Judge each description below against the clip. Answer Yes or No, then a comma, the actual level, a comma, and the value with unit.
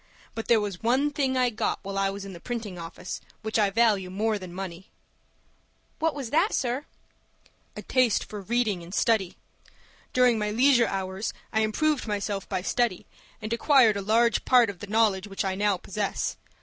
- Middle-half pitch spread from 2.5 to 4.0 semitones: Yes, average, 3.6 semitones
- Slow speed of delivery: No, average, 185 wpm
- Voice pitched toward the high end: Yes, high, 215 Hz